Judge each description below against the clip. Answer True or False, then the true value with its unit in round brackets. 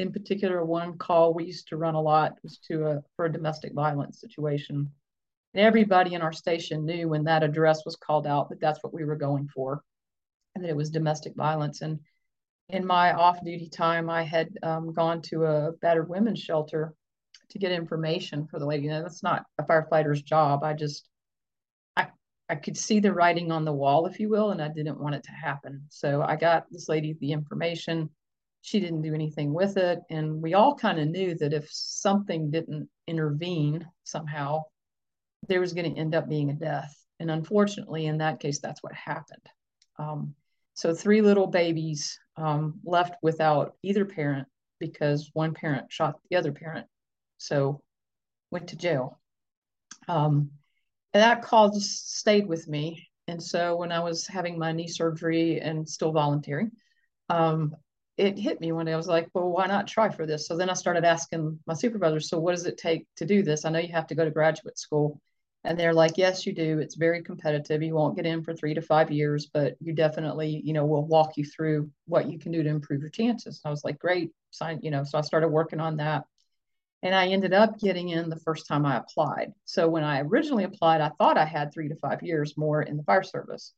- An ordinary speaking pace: False (210 wpm)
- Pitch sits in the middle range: True (160 Hz)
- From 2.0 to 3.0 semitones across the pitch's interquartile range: True (2.4 semitones)